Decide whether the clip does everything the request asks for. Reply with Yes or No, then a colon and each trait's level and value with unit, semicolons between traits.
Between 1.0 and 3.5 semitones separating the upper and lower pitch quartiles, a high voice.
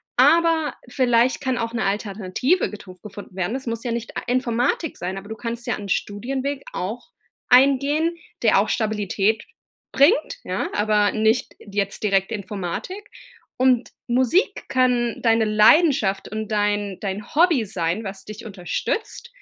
No: average, 4.0 semitones; high, 225 Hz